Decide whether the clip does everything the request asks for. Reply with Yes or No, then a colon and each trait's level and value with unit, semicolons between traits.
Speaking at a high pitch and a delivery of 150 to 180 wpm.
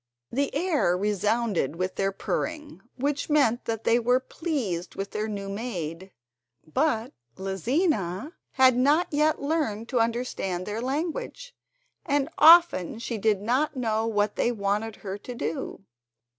No: high, 230 Hz; average, 140 wpm